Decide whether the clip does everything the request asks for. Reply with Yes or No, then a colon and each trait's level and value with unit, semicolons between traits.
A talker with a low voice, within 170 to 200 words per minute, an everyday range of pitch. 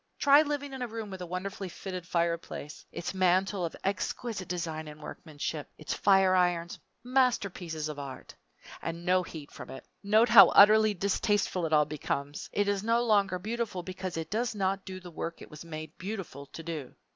No: medium, 185 Hz; average, 185 wpm; average, 3.9 semitones